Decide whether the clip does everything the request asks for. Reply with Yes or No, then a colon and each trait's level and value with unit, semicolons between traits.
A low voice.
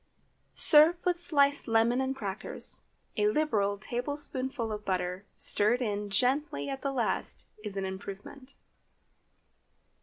No: high, 240 Hz